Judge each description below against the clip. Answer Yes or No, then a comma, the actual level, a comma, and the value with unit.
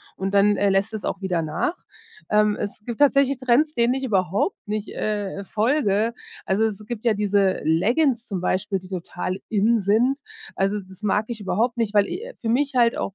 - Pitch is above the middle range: Yes, high, 210 Hz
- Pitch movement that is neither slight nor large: Yes, average, 3.4 semitones